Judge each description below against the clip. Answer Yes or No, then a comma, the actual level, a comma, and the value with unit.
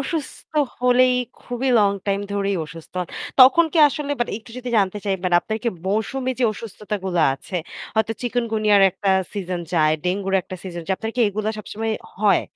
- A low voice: No, high, 210 Hz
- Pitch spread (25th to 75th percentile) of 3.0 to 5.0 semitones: Yes, average, 4.1 semitones